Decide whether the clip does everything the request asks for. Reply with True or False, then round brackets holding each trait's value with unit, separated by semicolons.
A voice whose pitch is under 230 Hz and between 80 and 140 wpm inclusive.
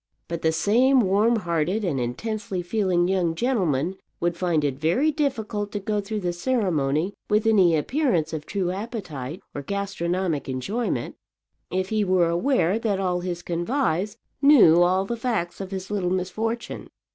False (185 Hz; 155 wpm)